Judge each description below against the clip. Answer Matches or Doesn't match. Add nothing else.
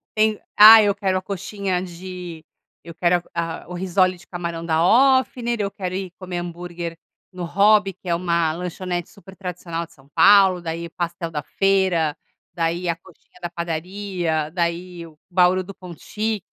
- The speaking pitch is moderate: Matches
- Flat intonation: Matches